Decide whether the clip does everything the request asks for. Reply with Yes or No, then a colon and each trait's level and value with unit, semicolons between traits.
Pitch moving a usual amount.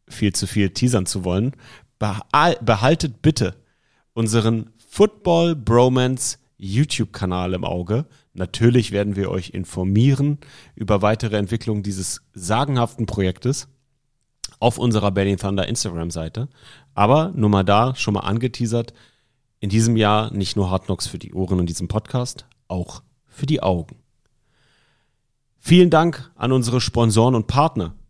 Yes: average, 4.4 semitones